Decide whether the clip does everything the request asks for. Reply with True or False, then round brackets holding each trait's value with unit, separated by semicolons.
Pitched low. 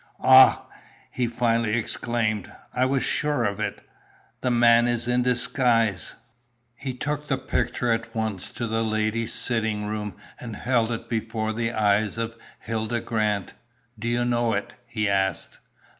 True (115 Hz)